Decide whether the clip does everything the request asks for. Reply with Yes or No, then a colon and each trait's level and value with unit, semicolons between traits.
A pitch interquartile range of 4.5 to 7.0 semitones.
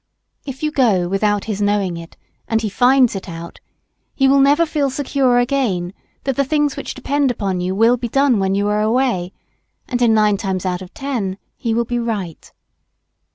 Yes: wide, 5.6 semitones